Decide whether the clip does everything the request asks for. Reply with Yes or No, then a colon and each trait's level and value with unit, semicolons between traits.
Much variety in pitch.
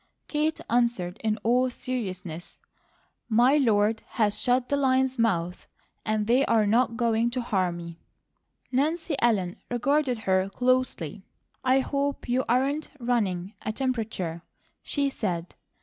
No: average, 4.5 semitones